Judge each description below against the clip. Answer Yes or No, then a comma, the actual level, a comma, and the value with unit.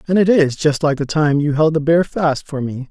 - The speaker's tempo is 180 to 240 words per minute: No, fast, 290 wpm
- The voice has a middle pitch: Yes, medium, 150 Hz